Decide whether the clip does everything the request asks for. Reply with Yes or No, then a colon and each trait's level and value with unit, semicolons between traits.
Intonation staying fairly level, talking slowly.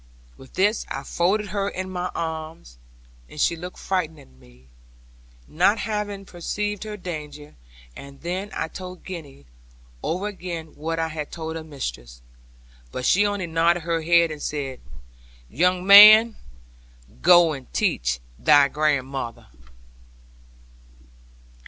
No: average, 4.2 semitones; slow, 130 wpm